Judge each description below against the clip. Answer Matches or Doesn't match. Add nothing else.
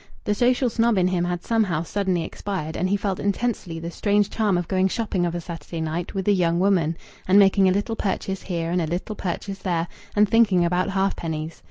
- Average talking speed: Doesn't match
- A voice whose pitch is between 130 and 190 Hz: Matches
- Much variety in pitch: Doesn't match